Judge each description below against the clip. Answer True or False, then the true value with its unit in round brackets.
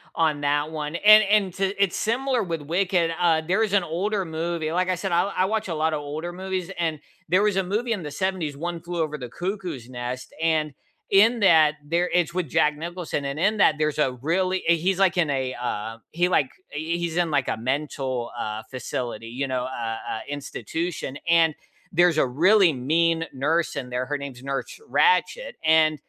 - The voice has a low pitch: False (165 Hz)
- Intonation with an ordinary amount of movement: True (4.2 semitones)